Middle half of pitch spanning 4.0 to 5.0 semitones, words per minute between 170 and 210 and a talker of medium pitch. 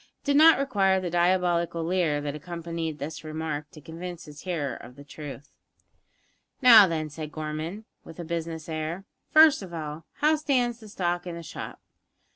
No: average, 3.3 semitones; average, 175 wpm; medium, 170 Hz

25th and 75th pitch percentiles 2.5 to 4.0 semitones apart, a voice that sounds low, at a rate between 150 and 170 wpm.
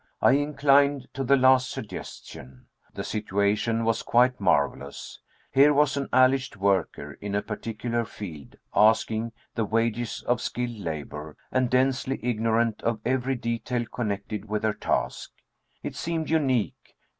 No: average, 3.7 semitones; low, 115 Hz; slow, 135 wpm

